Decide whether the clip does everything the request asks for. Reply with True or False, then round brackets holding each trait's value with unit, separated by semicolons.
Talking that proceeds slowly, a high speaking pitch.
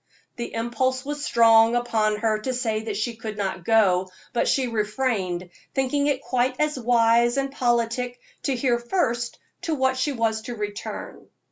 False (165 wpm; 235 Hz)